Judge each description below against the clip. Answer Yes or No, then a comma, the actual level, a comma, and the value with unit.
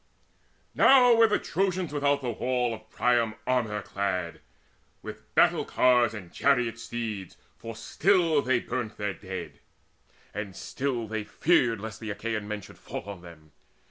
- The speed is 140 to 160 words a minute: Yes, average, 155 wpm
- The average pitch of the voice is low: Yes, low, 115 Hz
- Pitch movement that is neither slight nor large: Yes, average, 4.7 semitones